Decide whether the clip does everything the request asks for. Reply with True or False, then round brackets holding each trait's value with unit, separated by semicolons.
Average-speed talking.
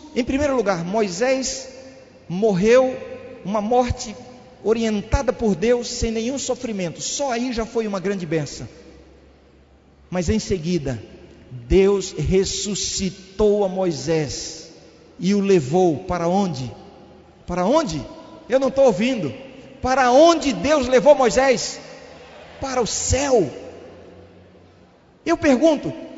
False (110 wpm)